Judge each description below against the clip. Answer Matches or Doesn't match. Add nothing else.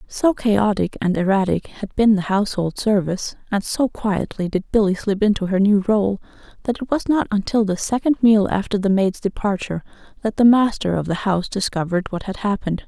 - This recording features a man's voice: Doesn't match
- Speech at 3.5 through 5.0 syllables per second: Doesn't match